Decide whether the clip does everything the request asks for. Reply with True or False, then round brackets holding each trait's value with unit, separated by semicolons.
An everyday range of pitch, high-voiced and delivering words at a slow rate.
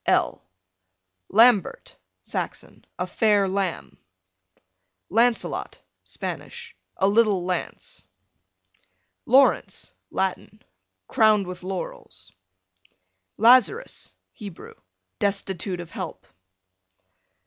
True (3.4 semitones; 200 Hz; 70 wpm)